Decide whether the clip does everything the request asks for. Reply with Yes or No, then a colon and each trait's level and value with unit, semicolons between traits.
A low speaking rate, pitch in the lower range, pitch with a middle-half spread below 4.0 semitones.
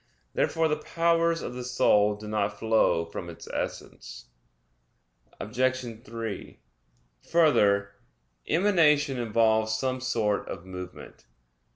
No: slow, 105 wpm; low, 115 Hz; wide, 5.4 semitones